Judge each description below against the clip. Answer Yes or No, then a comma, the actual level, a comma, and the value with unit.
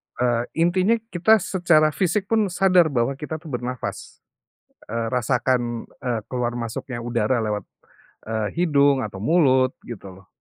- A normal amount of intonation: No, wide, 5.8 semitones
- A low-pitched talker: Yes, low, 130 Hz